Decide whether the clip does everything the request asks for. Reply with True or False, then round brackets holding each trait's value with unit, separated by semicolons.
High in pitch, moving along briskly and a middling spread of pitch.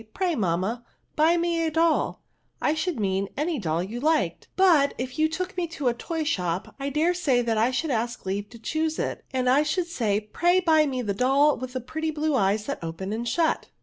False (275 Hz; 215 wpm; 6.6 semitones)